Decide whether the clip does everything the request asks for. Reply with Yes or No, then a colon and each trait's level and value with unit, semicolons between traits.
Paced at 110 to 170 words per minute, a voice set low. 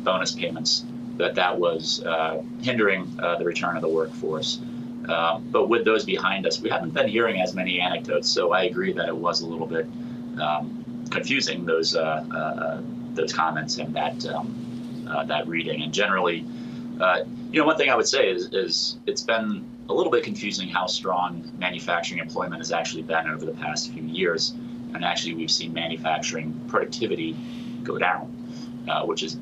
No: average, 180 wpm; very low, 90 Hz